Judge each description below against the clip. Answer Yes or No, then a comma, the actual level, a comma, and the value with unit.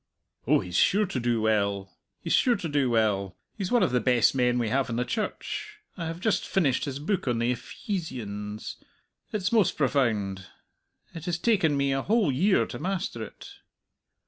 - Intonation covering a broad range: Yes, wide, 8.3 semitones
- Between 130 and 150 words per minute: No, average, 185 wpm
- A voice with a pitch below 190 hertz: Yes, low, 135 Hz